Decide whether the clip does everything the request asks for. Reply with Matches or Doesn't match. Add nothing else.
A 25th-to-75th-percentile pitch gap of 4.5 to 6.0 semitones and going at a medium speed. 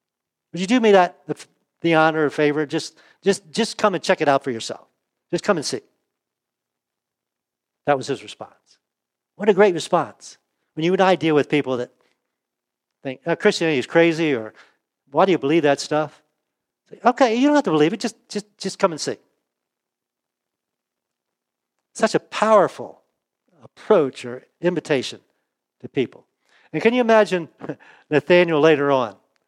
Matches